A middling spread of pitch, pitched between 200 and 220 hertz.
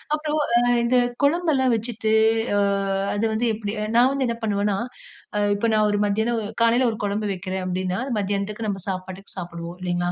Yes: average, 3.6 semitones; high, 210 Hz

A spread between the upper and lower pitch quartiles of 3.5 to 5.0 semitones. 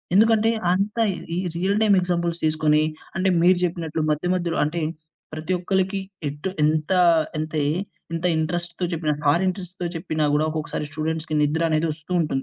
No: average, 2.9 semitones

